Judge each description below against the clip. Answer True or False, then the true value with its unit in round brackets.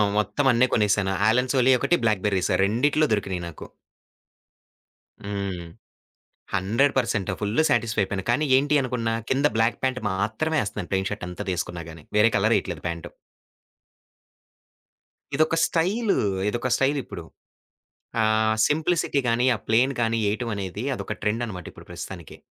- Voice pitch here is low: True (110 Hz)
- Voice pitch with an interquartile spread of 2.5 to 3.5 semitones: False (4.7 semitones)